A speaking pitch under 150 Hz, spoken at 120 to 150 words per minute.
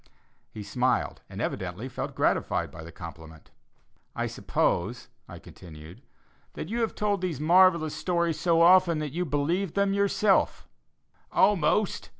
No: medium, 165 Hz; average, 140 wpm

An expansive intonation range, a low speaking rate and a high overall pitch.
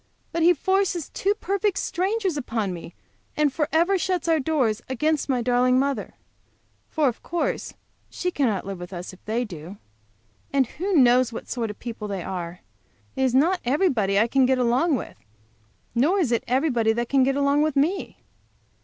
No: wide, 6.2 semitones; average, 175 wpm; very high, 265 Hz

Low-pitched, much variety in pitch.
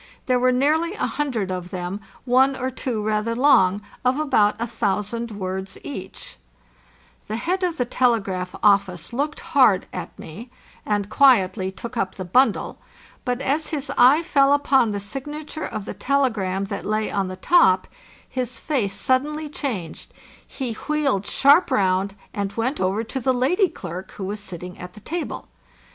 No: high, 230 Hz; wide, 5.9 semitones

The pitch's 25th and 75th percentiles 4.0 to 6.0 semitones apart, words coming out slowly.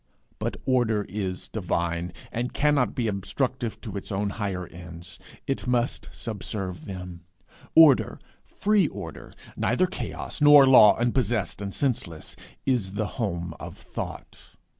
Yes: wide, 5.5 semitones; slow, 130 wpm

